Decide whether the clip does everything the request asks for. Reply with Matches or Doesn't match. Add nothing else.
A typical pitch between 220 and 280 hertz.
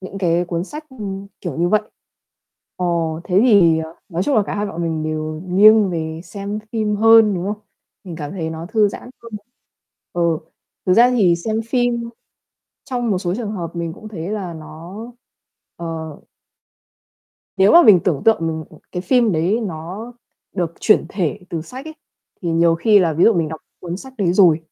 Doesn't match